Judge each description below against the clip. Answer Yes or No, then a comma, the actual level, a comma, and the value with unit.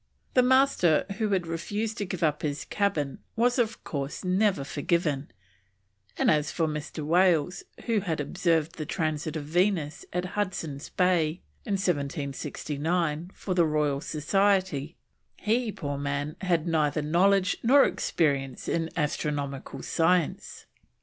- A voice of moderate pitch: Yes, medium, 165 Hz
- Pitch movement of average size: Yes, average, 4.2 semitones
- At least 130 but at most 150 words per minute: Yes, slow, 135 wpm